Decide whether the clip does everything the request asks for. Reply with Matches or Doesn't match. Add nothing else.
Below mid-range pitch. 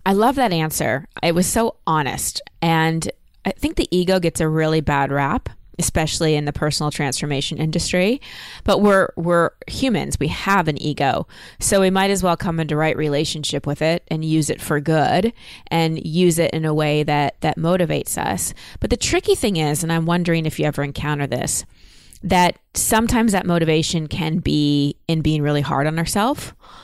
Doesn't match